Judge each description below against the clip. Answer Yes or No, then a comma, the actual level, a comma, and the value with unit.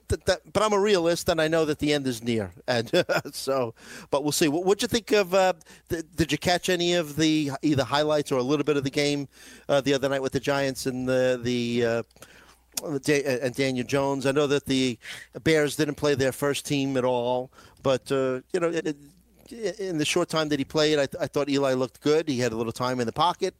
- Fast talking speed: Yes, fast, 235 wpm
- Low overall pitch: No, medium, 145 Hz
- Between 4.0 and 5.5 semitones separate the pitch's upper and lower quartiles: No, average, 3.3 semitones